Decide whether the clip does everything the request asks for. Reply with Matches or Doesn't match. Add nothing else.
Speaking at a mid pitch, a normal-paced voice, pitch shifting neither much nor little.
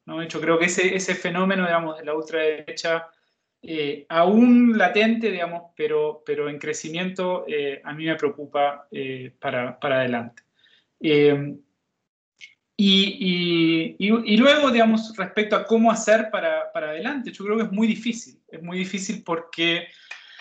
Doesn't match